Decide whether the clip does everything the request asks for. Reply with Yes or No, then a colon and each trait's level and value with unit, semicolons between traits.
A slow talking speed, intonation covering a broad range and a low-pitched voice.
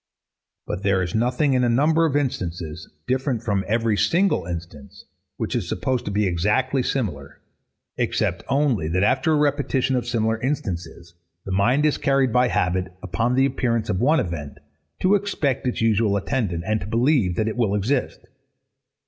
No: average, 170 wpm; wide, 6.1 semitones; low, 115 Hz